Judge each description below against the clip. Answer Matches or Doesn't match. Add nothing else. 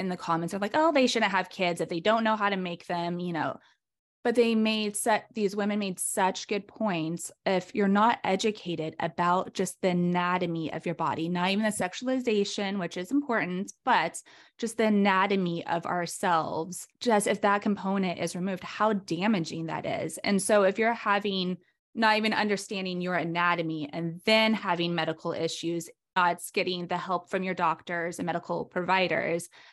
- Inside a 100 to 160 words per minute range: Doesn't match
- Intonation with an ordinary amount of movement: Matches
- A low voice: Doesn't match